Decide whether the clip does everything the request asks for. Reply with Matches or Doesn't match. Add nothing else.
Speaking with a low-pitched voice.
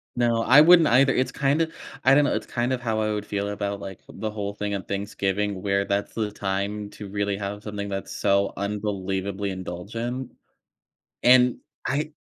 Matches